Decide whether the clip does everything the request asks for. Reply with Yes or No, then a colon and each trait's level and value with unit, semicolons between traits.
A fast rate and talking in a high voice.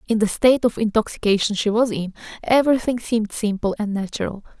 No: average, 170 wpm; high, 220 Hz